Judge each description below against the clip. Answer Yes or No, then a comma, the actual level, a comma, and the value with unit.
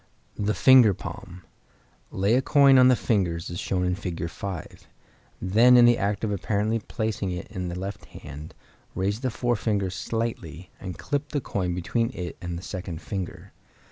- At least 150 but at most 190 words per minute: Yes, average, 170 wpm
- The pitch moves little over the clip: No, average, 4.4 semitones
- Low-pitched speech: Yes, low, 100 Hz